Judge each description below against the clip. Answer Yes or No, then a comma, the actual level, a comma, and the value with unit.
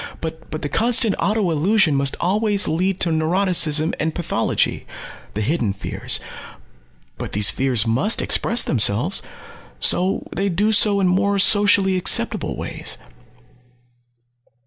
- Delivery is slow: Yes, slow, 125 wpm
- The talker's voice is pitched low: No, medium, 180 Hz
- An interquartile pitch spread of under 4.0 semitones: No, average, 4.8 semitones